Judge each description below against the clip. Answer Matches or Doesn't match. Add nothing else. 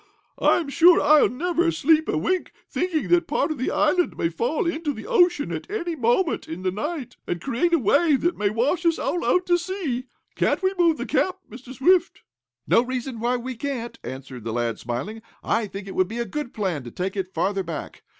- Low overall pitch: Doesn't match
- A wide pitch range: Matches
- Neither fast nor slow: Doesn't match